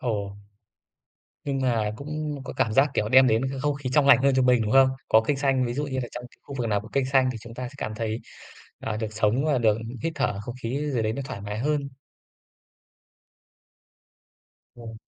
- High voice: No, low, 125 Hz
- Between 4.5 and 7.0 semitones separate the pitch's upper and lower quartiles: No, average, 3.8 semitones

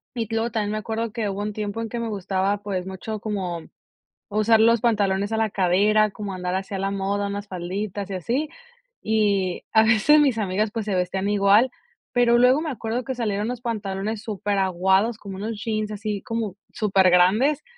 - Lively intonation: No, narrow, 2.5 semitones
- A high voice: Yes, high, 210 Hz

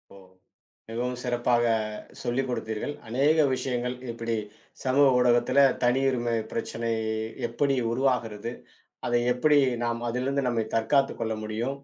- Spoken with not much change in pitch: Yes, narrow, 2.2 semitones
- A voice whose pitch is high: No, low, 120 Hz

